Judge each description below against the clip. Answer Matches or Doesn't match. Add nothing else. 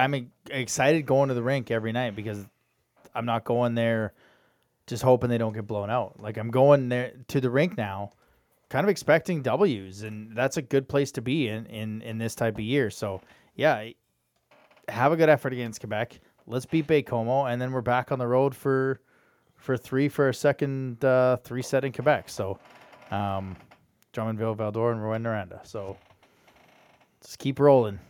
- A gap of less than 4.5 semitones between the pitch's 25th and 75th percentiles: Matches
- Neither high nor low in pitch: Doesn't match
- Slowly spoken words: Doesn't match